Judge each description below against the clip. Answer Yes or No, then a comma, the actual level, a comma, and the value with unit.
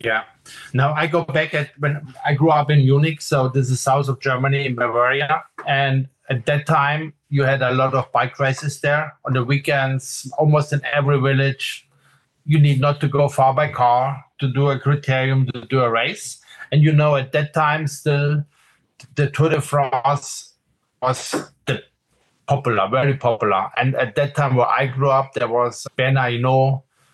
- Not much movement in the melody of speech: Yes, narrow, 2.0 semitones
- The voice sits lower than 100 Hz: No, medium, 140 Hz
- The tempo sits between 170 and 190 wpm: Yes, average, 185 wpm